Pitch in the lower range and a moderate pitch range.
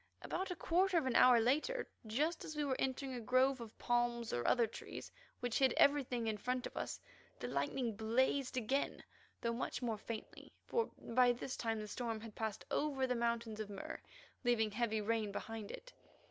No: high, 240 Hz; average, 3.0 semitones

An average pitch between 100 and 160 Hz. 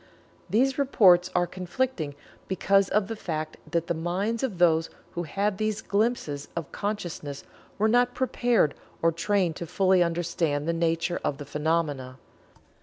No: medium, 175 Hz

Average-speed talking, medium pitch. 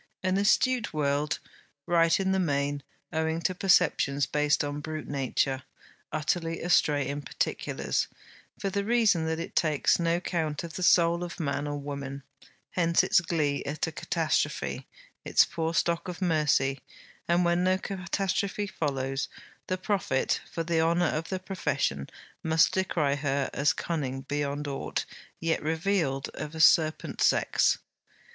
Yes: average, 150 wpm; medium, 160 Hz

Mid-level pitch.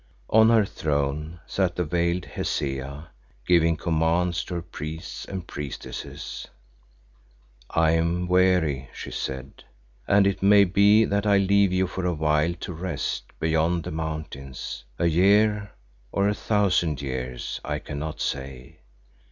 No: very low, 85 Hz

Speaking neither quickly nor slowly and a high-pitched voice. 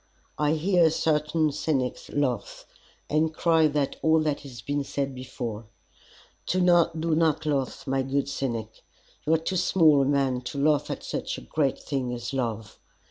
No: average, 160 wpm; medium, 145 Hz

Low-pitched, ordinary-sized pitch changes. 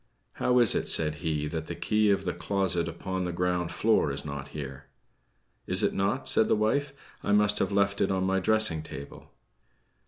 Yes: very low, 95 Hz; average, 4.7 semitones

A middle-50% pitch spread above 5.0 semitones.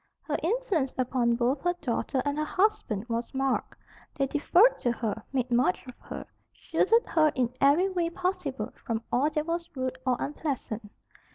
Yes: wide, 5.5 semitones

